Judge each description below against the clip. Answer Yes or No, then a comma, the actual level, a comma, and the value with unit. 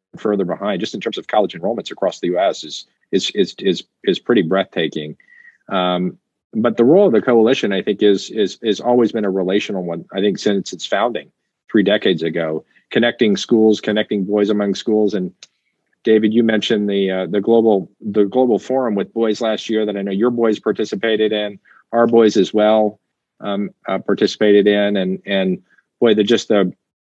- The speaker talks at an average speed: Yes, average, 190 wpm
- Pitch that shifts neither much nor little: No, narrow, 2.2 semitones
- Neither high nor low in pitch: No, low, 105 Hz